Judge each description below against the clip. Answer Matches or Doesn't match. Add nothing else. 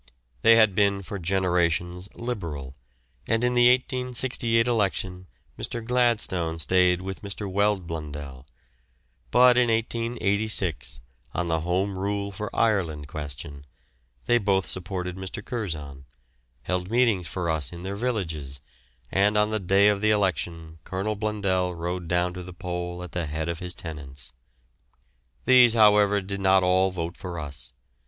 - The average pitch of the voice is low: Matches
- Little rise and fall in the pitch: Doesn't match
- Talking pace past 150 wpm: Doesn't match